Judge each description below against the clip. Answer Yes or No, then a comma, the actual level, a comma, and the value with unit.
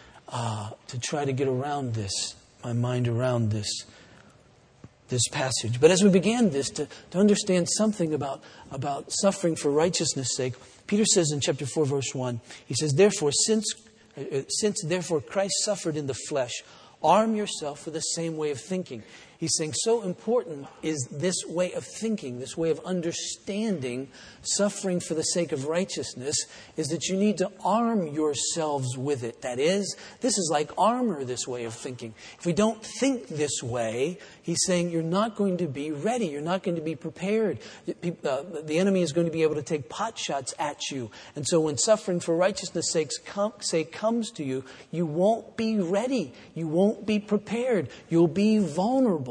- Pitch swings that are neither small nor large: No, wide, 6.0 semitones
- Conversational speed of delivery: Yes, average, 180 wpm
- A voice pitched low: No, medium, 165 Hz